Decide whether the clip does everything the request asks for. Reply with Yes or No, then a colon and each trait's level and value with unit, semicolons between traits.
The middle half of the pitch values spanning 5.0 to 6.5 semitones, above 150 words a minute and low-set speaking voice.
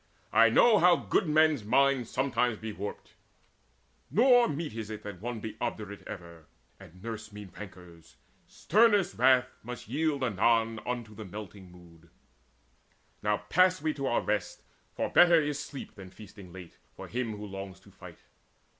Yes: wide, 5.6 semitones; average, 160 wpm; low, 110 Hz